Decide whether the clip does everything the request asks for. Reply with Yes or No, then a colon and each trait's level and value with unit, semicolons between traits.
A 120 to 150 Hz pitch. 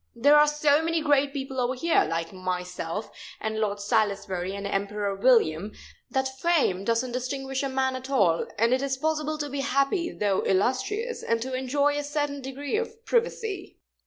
No: very high, 265 Hz